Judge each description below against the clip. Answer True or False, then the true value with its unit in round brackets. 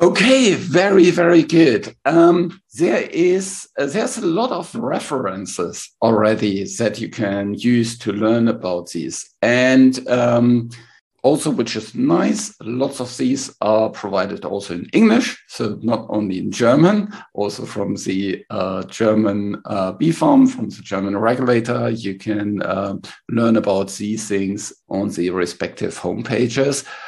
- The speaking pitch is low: True (115 Hz)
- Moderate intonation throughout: False (5.7 semitones)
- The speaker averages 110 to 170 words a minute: True (140 wpm)